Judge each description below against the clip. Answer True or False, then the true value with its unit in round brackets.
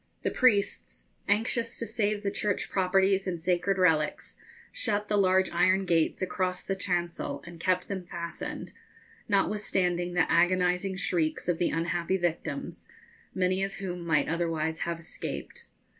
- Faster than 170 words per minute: False (145 wpm)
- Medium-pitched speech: True (180 Hz)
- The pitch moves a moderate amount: False (2.3 semitones)